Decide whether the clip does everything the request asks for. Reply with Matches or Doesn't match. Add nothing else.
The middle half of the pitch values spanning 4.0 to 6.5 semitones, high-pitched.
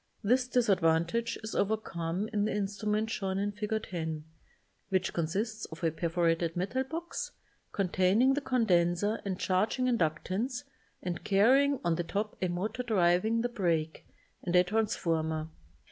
Matches